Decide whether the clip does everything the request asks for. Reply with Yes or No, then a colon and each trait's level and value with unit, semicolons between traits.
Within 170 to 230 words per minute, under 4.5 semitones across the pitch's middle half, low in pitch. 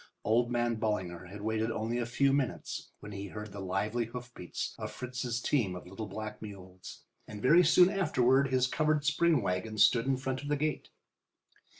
Yes: average, 185 wpm; average, 4.1 semitones; low, 115 Hz